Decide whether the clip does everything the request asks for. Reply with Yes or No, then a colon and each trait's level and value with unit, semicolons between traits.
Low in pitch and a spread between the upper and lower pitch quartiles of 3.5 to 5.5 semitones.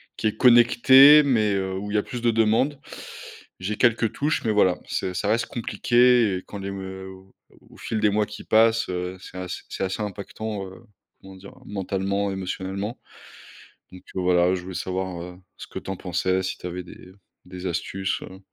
No: low, 100 Hz; average, 2.9 semitones